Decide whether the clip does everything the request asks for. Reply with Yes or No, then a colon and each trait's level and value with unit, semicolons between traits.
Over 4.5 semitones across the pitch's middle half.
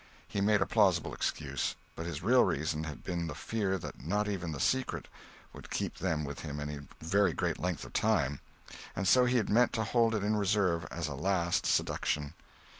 Yes: average, 5.1 semitones